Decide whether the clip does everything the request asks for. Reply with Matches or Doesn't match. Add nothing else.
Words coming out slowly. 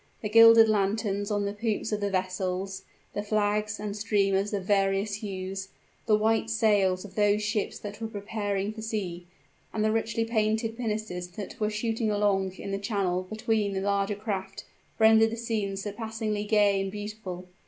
Doesn't match